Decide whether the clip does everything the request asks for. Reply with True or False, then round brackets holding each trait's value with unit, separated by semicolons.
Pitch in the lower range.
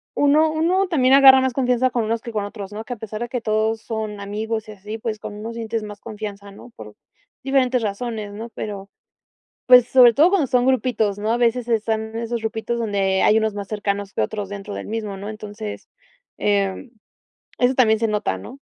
False (220 Hz)